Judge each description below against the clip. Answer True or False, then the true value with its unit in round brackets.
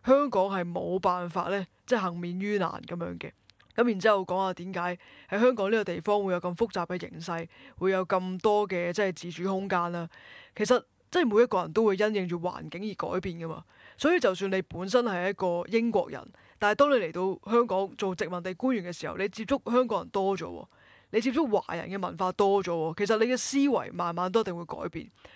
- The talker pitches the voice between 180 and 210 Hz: True (190 Hz)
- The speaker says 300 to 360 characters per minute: True (315 characters per minute)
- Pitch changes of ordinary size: True (3.8 semitones)